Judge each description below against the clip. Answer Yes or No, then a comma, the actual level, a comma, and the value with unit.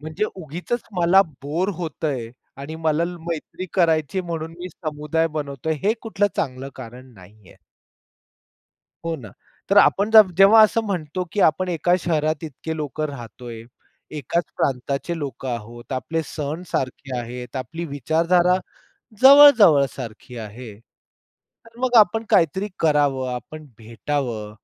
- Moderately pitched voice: Yes, medium, 155 Hz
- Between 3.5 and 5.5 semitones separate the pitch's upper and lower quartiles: Yes, average, 5.1 semitones